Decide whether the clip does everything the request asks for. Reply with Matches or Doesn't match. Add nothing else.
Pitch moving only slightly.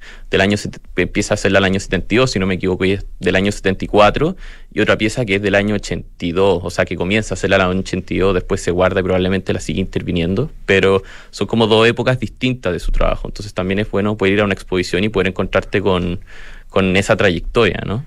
Matches